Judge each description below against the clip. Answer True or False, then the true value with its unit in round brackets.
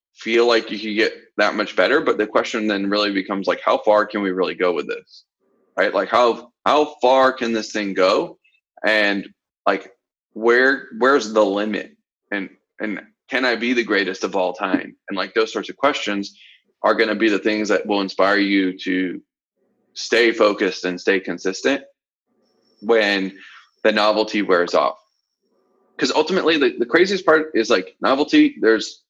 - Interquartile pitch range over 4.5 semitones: True (5.4 semitones)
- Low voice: True (110 Hz)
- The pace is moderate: True (175 wpm)